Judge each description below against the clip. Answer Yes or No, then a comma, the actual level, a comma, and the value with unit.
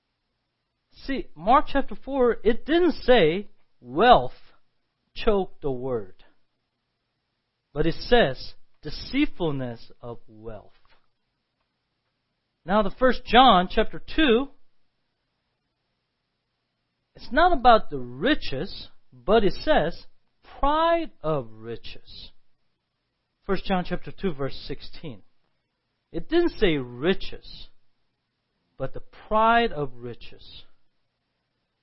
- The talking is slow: Yes, slow, 90 wpm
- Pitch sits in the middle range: Yes, medium, 180 Hz